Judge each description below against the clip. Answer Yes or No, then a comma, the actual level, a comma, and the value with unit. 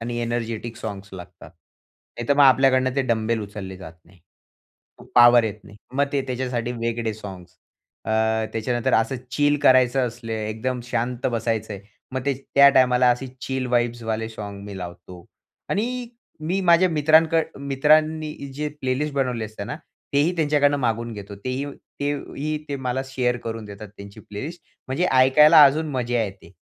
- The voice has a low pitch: Yes, low, 125 Hz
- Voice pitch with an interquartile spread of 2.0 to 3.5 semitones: No, average, 4.1 semitones